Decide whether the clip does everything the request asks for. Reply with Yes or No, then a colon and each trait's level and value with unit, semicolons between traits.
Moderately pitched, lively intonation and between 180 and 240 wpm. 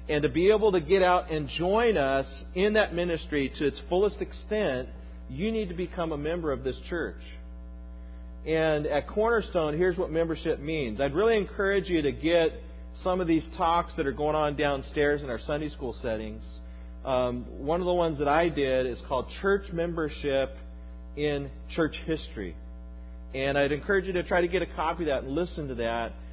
Yes: medium, 150 Hz; wide, 6.2 semitones; average, 190 wpm